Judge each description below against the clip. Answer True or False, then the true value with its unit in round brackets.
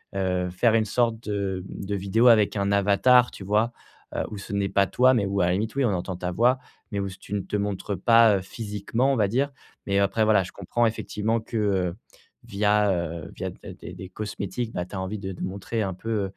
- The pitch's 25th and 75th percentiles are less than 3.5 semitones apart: True (2.7 semitones)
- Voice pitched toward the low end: True (100 Hz)